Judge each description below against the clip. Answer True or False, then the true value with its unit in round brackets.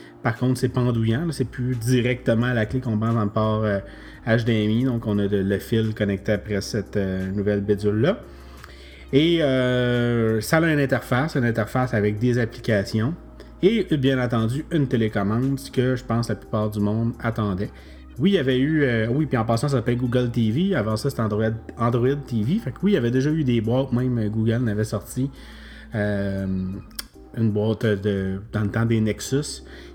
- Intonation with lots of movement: False (3.3 semitones)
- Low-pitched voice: True (115 Hz)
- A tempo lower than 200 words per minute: True (190 wpm)